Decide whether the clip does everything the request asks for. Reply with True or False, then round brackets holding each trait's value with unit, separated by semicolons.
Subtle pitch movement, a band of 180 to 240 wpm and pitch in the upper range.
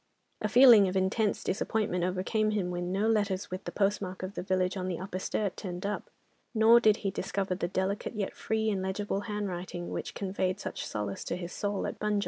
True (2.2 semitones; 205 wpm; 195 Hz)